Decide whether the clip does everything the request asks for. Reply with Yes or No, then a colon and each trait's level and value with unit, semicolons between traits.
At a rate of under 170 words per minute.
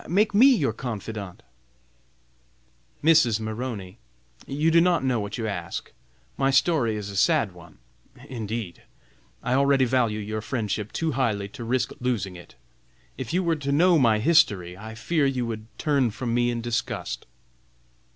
Yes: average, 155 wpm